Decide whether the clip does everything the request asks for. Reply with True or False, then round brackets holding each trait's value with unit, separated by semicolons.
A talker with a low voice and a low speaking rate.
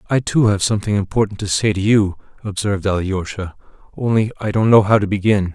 False (100 Hz; 195 wpm)